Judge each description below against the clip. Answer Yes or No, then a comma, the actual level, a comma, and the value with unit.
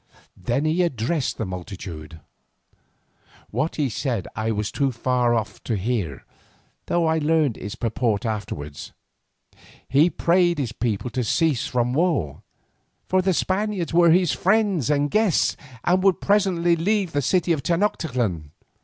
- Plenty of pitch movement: Yes, wide, 7.6 semitones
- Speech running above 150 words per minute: No, average, 145 wpm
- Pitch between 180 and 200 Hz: No, medium, 140 Hz